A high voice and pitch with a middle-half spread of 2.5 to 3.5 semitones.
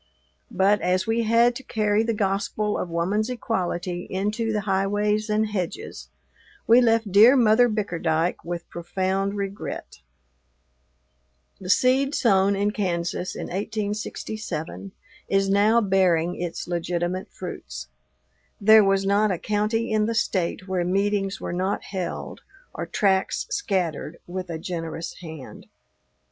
Yes: high, 195 Hz; average, 3.1 semitones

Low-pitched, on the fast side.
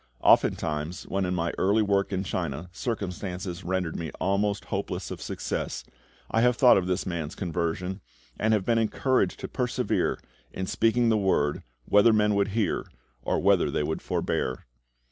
No: very low, 95 Hz; average, 165 wpm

